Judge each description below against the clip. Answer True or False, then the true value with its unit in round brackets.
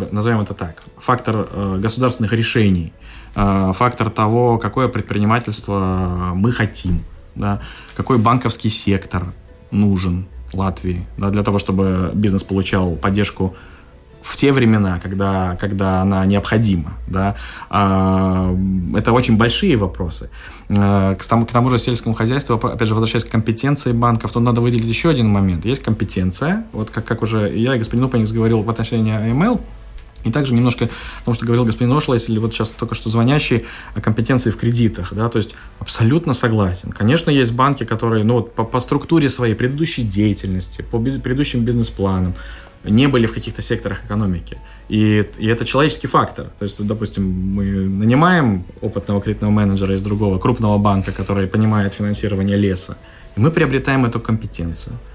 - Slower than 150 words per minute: False (155 wpm)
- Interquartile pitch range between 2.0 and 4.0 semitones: True (3.3 semitones)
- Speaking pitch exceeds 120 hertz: False (110 Hz)